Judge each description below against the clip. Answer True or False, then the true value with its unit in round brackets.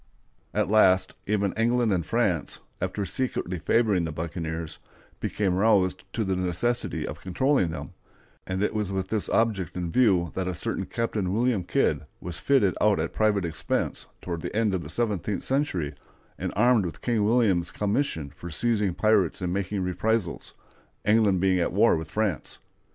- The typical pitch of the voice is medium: False (95 Hz)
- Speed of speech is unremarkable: True (165 wpm)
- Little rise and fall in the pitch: False (3.6 semitones)